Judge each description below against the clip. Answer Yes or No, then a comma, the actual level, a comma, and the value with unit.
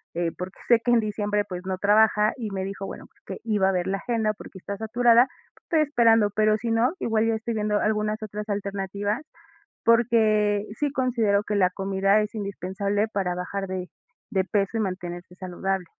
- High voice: Yes, high, 210 Hz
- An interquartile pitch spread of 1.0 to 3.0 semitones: Yes, narrow, 2.4 semitones